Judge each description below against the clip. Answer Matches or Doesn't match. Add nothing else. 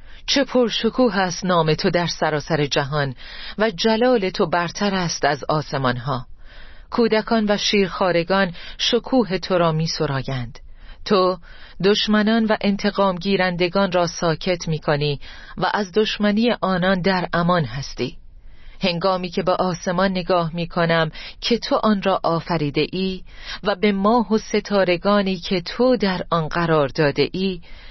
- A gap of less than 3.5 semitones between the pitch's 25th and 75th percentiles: Doesn't match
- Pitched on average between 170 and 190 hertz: Matches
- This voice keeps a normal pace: Matches